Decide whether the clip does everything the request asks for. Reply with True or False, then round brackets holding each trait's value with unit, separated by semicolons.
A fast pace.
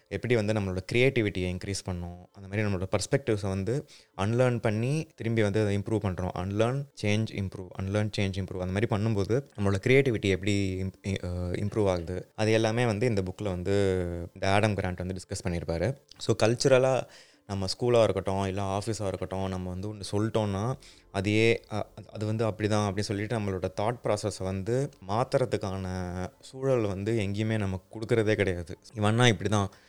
True (155 wpm)